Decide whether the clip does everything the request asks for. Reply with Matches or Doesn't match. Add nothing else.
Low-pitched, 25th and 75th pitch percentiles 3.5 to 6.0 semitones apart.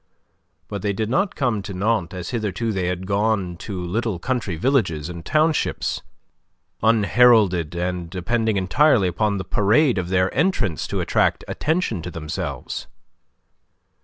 Matches